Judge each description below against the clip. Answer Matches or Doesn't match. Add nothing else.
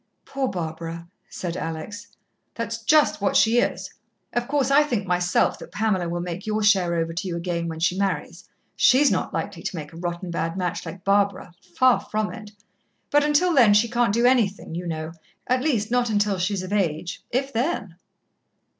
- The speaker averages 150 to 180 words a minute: Doesn't match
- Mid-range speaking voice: Doesn't match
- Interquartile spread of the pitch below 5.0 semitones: Doesn't match